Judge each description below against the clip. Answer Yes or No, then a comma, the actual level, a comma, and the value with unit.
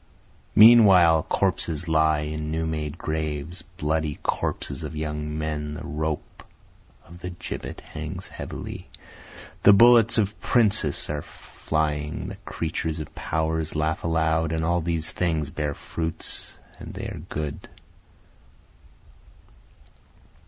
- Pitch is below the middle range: Yes, very low, 80 Hz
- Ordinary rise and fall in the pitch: No, narrow, 1.8 semitones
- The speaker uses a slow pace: Yes, slow, 120 wpm